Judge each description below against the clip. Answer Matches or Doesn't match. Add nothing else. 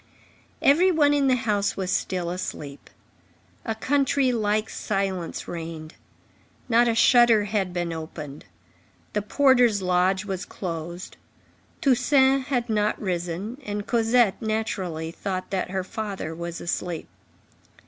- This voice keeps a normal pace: Doesn't match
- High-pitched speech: Matches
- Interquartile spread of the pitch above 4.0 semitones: Matches